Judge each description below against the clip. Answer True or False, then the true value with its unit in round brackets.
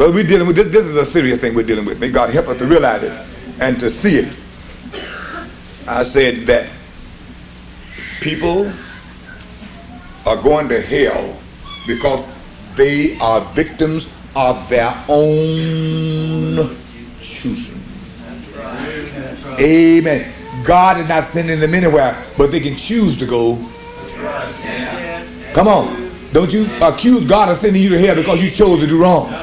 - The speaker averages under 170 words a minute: True (145 wpm)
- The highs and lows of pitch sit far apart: True (6.0 semitones)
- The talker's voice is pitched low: False (160 Hz)